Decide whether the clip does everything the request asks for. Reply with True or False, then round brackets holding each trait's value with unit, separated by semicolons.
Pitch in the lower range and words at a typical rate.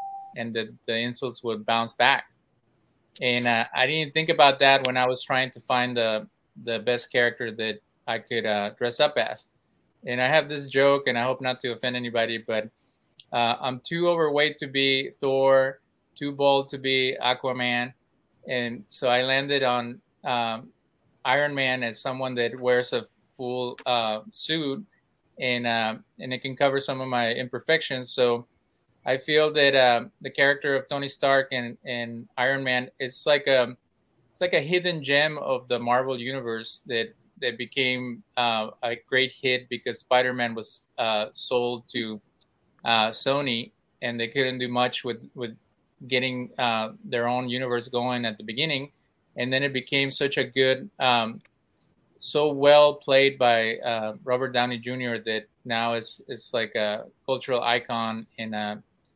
True (125 Hz; 165 wpm)